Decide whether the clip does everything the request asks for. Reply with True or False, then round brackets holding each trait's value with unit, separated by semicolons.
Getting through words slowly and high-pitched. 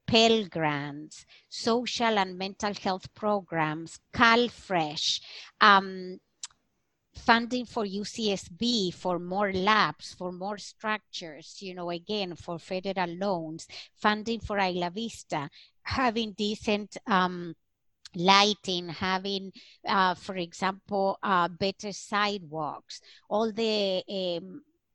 True (100 wpm; 195 Hz)